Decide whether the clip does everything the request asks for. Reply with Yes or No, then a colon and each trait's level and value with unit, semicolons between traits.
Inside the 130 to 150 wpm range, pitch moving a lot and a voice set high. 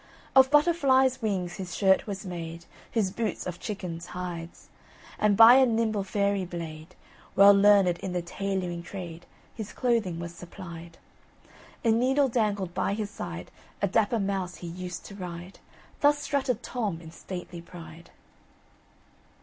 No: average, 145 wpm; average, 4.2 semitones; high, 195 Hz